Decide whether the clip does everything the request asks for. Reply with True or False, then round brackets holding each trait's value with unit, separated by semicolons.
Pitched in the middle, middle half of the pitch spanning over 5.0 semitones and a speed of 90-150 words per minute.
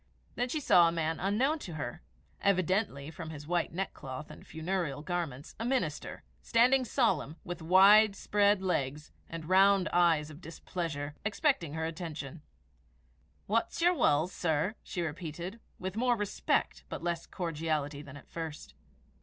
False (175 Hz; 4.3 semitones; 145 wpm)